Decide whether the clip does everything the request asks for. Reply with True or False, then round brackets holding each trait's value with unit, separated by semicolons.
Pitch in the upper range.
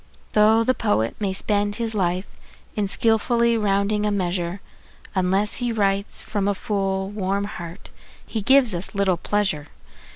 True (205 Hz)